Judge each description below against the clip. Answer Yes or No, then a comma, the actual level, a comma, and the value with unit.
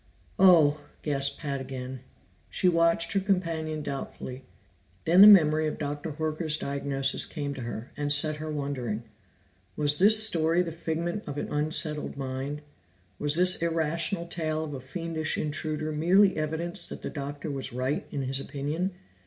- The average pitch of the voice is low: No, medium, 155 Hz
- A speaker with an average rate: Yes, average, 155 wpm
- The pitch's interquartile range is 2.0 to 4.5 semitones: Yes, average, 2.9 semitones